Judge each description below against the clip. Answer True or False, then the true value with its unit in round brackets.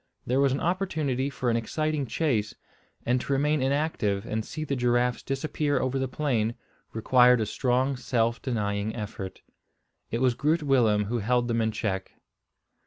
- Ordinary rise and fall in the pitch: True (3.7 semitones)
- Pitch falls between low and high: False (125 Hz)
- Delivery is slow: False (165 wpm)